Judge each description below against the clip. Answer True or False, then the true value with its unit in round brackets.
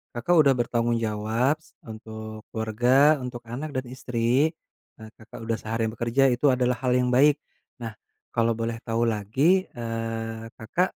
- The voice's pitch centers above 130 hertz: False (115 Hz)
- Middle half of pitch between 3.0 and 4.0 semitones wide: False (2.5 semitones)